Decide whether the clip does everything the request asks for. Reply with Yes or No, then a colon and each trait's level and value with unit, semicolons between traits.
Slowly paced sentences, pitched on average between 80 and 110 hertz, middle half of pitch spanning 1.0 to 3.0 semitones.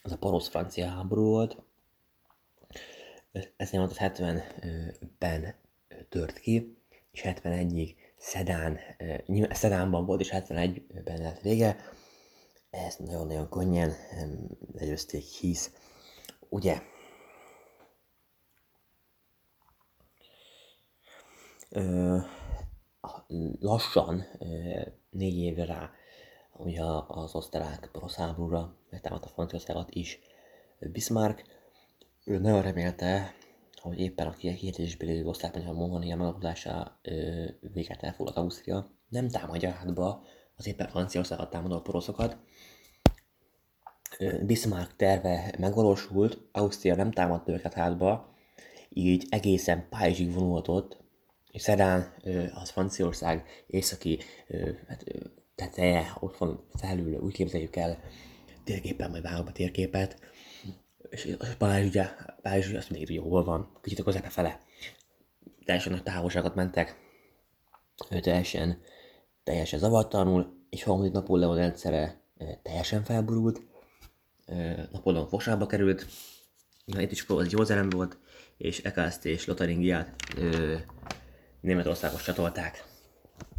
Yes: slow, 95 wpm; very low, 90 Hz; narrow, 2.4 semitones